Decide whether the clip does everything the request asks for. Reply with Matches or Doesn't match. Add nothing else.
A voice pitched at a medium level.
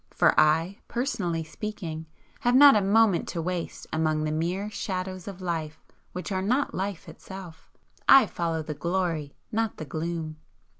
Matches